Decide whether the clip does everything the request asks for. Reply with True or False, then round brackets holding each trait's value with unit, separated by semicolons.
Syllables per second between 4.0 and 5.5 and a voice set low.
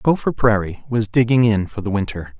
True (5.2 syllables/s; 110 Hz)